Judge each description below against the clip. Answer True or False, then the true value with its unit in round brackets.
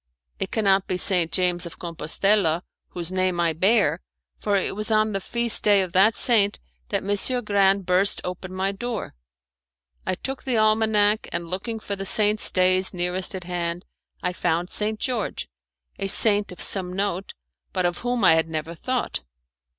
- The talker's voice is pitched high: True (195 Hz)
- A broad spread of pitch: False (2.9 semitones)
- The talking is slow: False (175 wpm)